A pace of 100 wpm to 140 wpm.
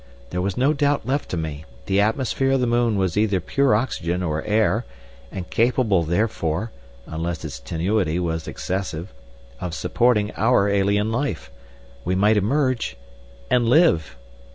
Yes: slow, 135 wpm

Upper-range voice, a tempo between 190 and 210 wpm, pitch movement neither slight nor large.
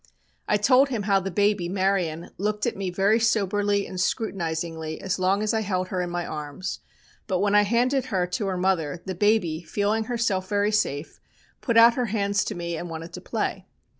Yes: high, 195 Hz; average, 200 wpm; average, 3.2 semitones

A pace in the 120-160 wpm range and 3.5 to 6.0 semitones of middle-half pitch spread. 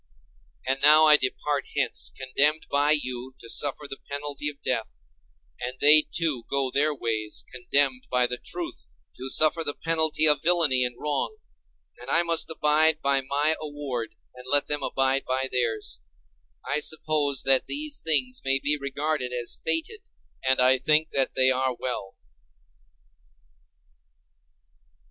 No: average, 140 wpm; average, 3.0 semitones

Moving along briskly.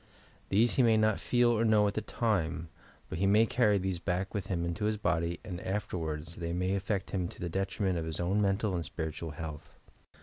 Yes: fast, 225 wpm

